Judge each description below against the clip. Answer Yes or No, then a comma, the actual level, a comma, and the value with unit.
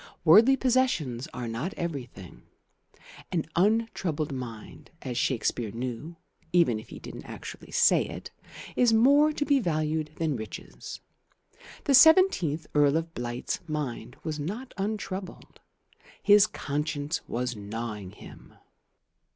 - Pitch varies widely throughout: Yes, wide, 8.9 semitones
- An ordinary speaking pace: No, slow, 125 wpm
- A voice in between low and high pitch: Yes, medium, 155 Hz